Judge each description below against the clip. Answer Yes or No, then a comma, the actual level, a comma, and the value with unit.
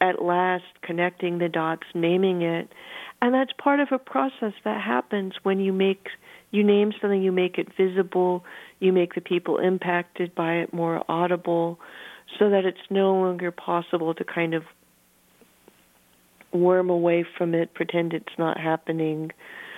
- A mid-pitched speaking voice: Yes, medium, 180 Hz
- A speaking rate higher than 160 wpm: No, average, 155 wpm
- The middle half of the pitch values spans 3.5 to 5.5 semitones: No, narrow, 2.5 semitones